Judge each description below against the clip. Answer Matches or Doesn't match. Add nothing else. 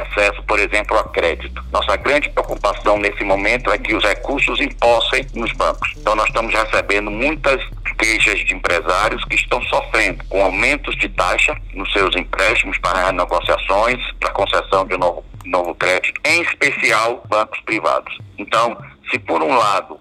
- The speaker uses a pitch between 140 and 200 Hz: Doesn't match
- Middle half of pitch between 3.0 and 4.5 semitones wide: Doesn't match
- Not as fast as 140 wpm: Doesn't match